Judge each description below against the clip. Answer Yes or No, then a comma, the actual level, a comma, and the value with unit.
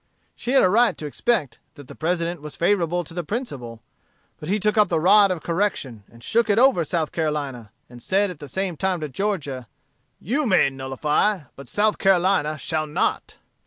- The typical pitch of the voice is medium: Yes, medium, 170 Hz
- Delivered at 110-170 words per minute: No, average, 195 wpm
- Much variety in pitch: Yes, wide, 5.7 semitones